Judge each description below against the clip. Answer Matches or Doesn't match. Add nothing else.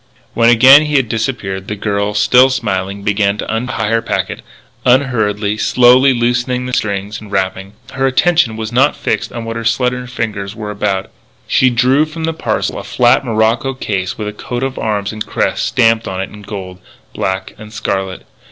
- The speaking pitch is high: Doesn't match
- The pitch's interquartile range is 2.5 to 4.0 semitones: Matches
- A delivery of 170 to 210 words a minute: Matches